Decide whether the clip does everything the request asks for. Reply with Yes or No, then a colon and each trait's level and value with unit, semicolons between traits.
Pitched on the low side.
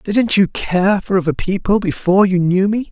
No: high, 195 Hz